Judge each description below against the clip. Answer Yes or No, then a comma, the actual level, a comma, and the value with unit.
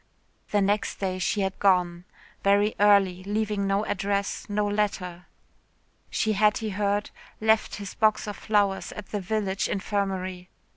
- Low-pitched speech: No, high, 200 Hz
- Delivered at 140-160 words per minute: Yes, average, 145 wpm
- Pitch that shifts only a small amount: Yes, narrow, 1.5 semitones